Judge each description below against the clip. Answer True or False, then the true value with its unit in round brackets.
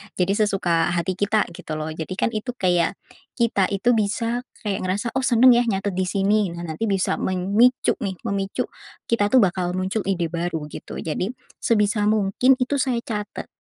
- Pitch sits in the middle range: False (200 Hz)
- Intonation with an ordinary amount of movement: True (3.7 semitones)